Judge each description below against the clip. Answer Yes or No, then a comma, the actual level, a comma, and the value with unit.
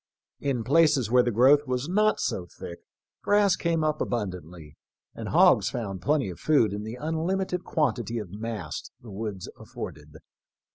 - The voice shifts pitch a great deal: Yes, wide, 7.5 semitones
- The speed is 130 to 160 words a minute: Yes, average, 155 wpm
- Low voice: Yes, low, 120 Hz